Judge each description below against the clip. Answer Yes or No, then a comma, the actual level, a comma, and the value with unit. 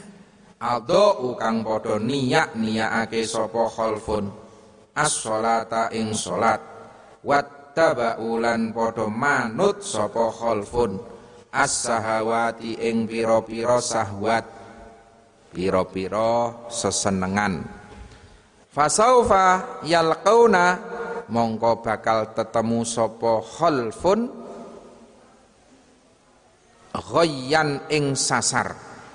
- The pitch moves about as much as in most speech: Yes, average, 4.3 semitones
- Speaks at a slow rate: Yes, slow, 65 wpm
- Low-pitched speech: Yes, low, 115 Hz